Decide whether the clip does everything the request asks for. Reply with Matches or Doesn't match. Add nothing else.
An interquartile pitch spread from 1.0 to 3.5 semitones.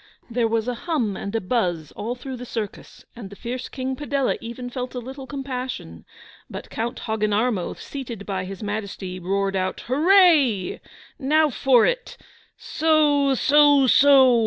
Doesn't match